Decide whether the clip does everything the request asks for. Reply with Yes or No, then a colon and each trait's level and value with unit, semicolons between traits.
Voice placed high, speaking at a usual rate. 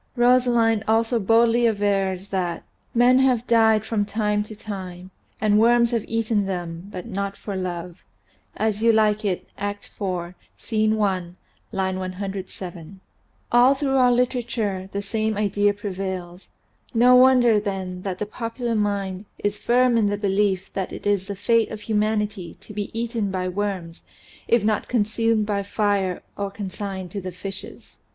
Yes: high, 205 Hz; average, 160 wpm